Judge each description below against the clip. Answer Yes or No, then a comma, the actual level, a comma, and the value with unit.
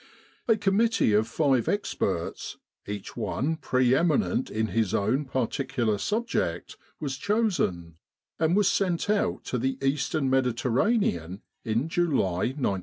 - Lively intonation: Yes, wide, 8.2 semitones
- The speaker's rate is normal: No, slow, 130 wpm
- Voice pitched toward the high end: No, low, 135 Hz